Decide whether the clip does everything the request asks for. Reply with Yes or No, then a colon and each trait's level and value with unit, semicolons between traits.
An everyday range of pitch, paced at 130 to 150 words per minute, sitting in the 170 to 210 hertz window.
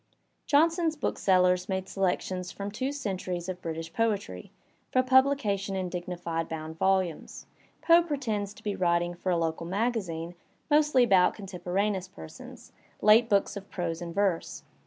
Yes: average, 4.2 semitones; average, 140 wpm; high, 190 Hz